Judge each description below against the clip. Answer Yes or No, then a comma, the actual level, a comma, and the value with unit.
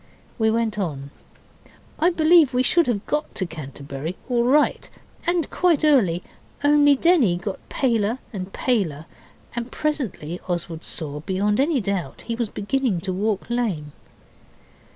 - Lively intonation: Yes, wide, 7.4 semitones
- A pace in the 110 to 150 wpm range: Yes, average, 145 wpm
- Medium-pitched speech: No, high, 220 Hz